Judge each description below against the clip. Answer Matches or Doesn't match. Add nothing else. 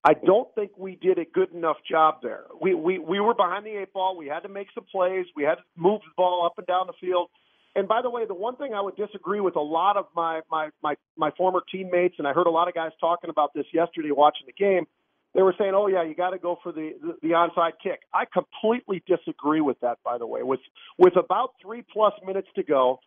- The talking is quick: Matches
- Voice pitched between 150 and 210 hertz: Matches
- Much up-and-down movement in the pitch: Doesn't match